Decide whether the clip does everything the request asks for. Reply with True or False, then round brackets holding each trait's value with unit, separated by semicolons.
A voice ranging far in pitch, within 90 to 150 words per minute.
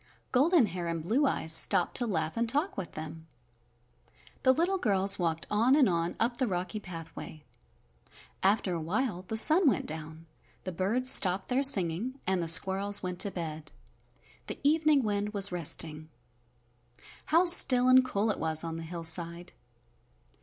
False (7.1 semitones; 160 wpm)